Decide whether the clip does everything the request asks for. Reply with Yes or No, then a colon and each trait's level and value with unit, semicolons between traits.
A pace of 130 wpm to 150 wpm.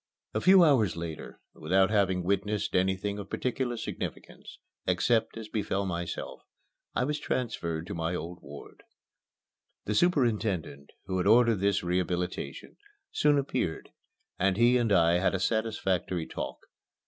Yes: average, 145 wpm